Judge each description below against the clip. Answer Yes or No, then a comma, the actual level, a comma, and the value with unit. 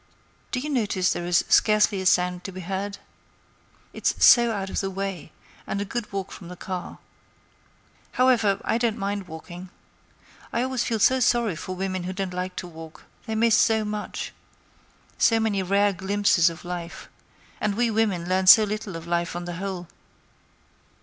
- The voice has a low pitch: No, high, 195 Hz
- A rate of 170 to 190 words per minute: Yes, average, 175 wpm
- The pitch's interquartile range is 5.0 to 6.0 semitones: No, average, 3.2 semitones